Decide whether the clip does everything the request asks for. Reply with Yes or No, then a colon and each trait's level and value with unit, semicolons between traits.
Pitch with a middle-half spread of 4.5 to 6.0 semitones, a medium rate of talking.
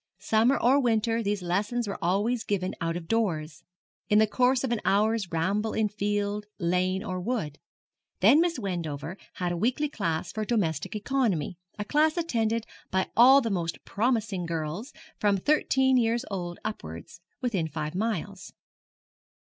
Yes: average, 4.8 semitones; average, 155 wpm